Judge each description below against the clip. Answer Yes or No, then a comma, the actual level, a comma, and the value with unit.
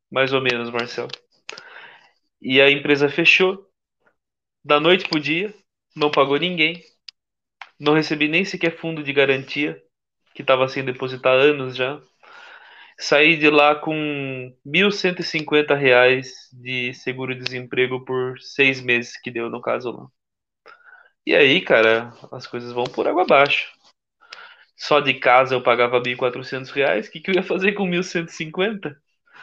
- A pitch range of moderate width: Yes, average, 4.6 semitones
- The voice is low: No, medium, 145 Hz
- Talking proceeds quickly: No, average, 150 wpm